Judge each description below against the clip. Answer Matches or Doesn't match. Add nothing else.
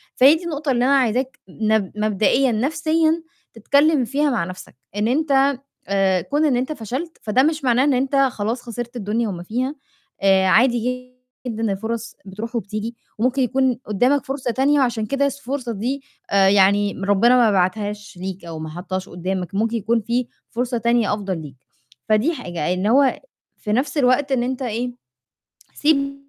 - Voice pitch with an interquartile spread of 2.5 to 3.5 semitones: Doesn't match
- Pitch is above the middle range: Matches